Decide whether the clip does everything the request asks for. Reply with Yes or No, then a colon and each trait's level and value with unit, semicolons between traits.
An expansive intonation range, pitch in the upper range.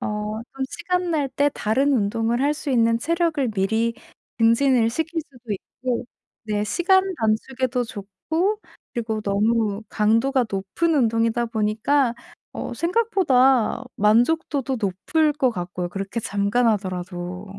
No: average, 5.0 semitones; high, 230 Hz